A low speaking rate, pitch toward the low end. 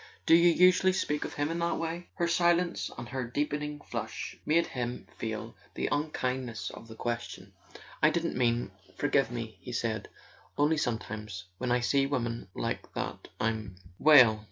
No: average, 170 wpm; low, 130 Hz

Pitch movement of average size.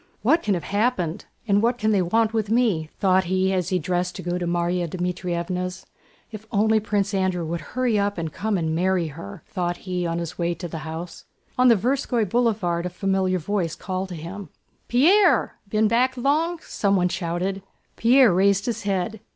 Yes: average, 3.7 semitones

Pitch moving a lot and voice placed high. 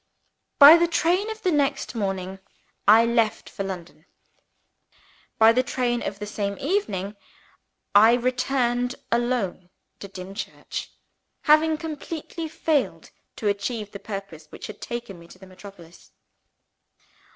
Yes: wide, 5.8 semitones; high, 230 Hz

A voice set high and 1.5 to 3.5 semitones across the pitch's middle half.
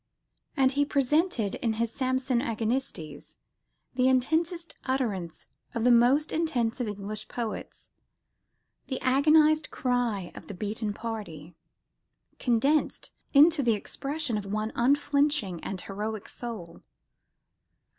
No: high, 245 Hz; average, 4.7 semitones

